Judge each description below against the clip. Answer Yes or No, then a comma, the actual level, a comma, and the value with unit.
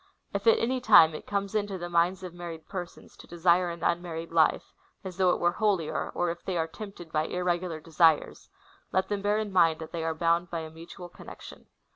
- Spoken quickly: Yes, fast, 225 wpm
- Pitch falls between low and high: Yes, medium, 175 Hz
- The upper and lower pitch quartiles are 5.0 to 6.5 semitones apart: No, narrow, 2.5 semitones